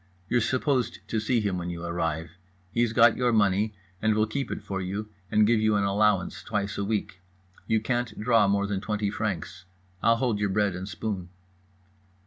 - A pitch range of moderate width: No, narrow, 2.3 semitones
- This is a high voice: No, low, 105 Hz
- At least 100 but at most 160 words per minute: No, average, 190 wpm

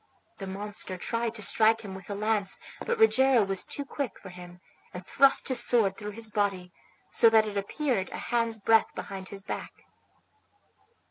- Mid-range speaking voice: No, high, 210 Hz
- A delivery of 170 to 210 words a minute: Yes, average, 180 wpm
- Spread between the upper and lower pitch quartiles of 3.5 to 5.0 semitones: No, average, 3.1 semitones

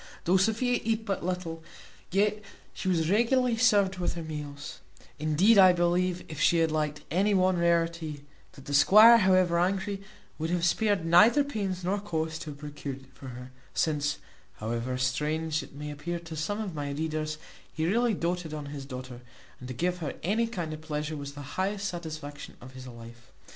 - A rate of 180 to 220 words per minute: Yes, average, 185 wpm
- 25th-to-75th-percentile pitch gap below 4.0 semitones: No, average, 4.3 semitones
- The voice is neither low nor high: Yes, medium, 165 Hz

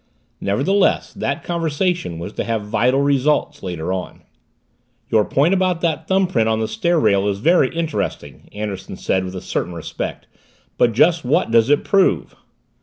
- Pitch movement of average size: No, wide, 8.6 semitones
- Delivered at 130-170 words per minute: Yes, average, 160 wpm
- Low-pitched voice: Yes, low, 125 Hz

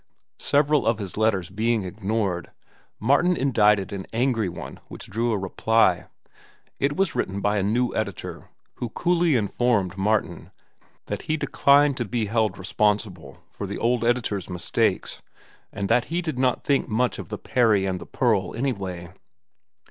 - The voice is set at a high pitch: No, low, 110 Hz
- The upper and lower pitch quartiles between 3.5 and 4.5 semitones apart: Yes, average, 4.2 semitones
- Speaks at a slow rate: No, average, 155 wpm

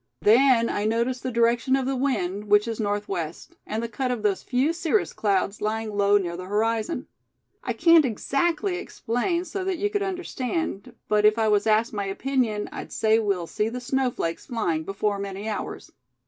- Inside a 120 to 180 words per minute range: No, average, 190 wpm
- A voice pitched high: Yes, high, 225 Hz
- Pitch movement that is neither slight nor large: Yes, average, 4.4 semitones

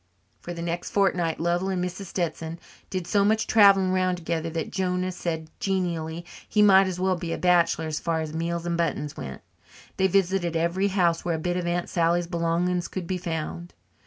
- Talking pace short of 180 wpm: No, average, 195 wpm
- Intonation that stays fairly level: Yes, narrow, 1.8 semitones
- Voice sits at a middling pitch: Yes, medium, 175 Hz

